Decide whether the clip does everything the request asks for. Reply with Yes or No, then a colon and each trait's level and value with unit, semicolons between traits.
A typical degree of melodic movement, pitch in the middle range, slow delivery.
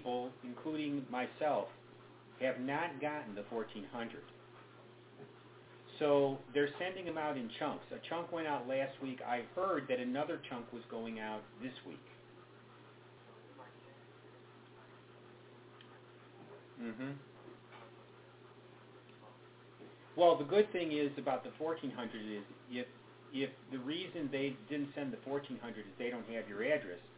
No: average, 4.4 semitones; low, 130 Hz; slow, 120 wpm